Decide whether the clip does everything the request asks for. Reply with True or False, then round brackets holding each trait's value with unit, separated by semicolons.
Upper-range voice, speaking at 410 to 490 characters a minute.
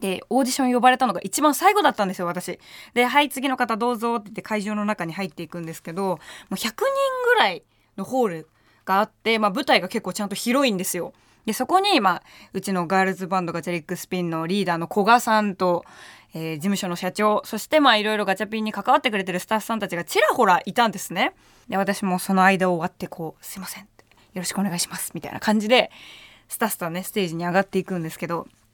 True (195 Hz; 480 characters per minute)